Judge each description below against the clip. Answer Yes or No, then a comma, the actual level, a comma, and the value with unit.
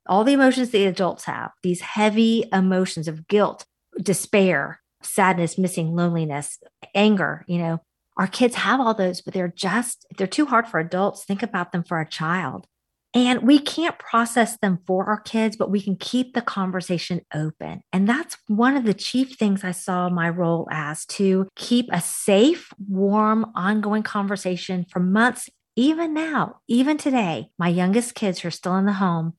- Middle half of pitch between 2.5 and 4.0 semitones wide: No, average, 4.4 semitones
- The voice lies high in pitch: Yes, high, 195 Hz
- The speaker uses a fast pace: No, average, 165 wpm